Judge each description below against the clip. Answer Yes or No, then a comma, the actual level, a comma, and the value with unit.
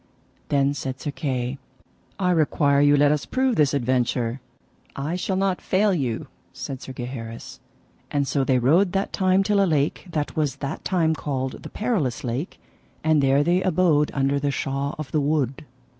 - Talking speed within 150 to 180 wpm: Yes, average, 175 wpm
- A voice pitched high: No, medium, 145 Hz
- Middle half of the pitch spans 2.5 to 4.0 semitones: No, average, 4.4 semitones